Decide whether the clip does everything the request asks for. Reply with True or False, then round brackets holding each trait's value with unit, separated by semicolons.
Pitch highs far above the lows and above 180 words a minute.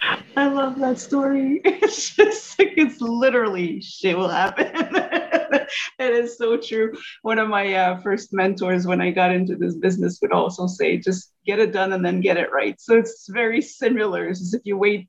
True (6.6 semitones; 190 wpm)